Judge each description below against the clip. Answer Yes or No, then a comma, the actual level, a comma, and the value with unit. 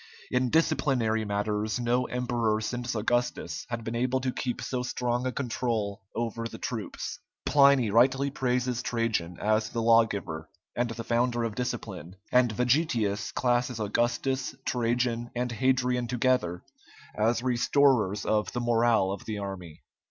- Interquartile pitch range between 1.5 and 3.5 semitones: Yes, narrow, 2.4 semitones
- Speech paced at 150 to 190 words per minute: No, average, 140 wpm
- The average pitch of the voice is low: Yes, low, 120 Hz